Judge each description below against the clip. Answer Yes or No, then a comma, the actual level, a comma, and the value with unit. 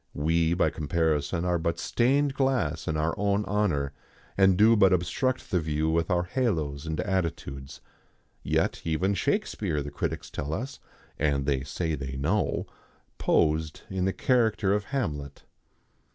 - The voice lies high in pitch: No, very low, 85 Hz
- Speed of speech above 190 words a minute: No, average, 150 wpm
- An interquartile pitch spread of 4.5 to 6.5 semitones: Yes, average, 5.2 semitones